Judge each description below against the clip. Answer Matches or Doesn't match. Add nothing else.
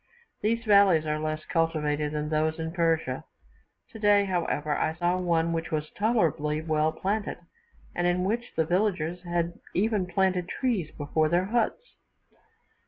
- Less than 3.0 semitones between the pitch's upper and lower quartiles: Doesn't match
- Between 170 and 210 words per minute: Doesn't match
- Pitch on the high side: Doesn't match